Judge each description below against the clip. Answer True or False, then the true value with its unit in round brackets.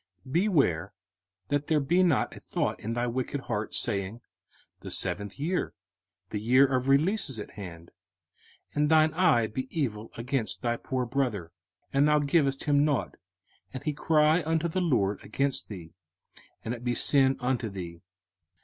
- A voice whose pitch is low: True (130 Hz)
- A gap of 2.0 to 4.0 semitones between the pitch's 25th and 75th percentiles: False (5.2 semitones)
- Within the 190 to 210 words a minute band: False (165 wpm)